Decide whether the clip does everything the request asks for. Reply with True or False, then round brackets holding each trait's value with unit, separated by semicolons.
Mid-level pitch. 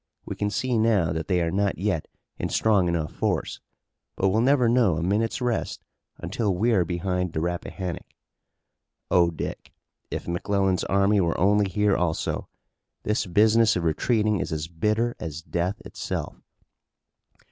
False (95 Hz)